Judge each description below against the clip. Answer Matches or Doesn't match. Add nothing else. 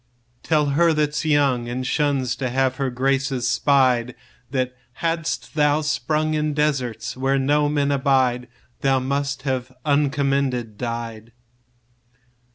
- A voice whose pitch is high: Doesn't match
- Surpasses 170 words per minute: Doesn't match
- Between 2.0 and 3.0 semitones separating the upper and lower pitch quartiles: Matches